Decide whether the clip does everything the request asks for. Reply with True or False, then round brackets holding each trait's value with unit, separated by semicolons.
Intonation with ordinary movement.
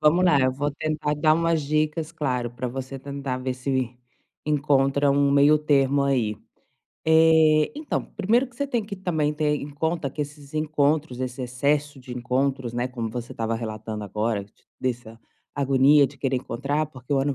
True (3.2 semitones)